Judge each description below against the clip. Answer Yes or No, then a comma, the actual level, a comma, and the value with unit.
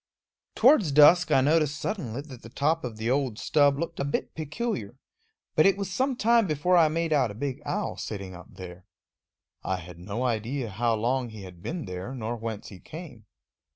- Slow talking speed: No, average, 195 wpm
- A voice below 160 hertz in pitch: Yes, low, 135 Hz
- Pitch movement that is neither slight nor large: No, wide, 6.7 semitones